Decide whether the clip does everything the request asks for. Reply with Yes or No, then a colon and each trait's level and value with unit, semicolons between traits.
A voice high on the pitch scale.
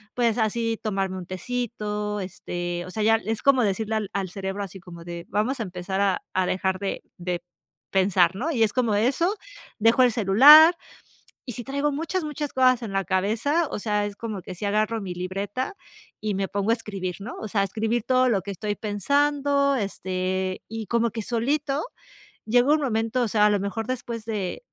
Yes: high, 215 Hz